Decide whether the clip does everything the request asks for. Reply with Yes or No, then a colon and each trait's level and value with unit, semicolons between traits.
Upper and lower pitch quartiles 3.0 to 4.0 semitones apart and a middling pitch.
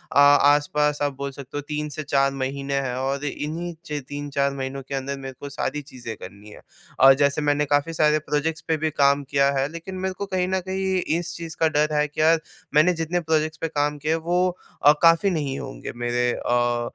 No: narrow, 2.6 semitones; medium, 145 Hz